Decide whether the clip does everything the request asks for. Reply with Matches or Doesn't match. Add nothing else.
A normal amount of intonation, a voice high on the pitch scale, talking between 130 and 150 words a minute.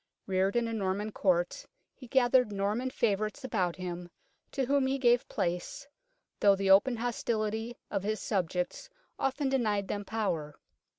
Matches